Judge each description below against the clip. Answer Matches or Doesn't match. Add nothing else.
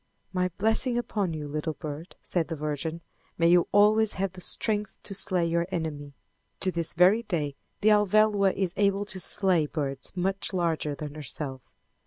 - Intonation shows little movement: Doesn't match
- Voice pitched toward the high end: Doesn't match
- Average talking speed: Matches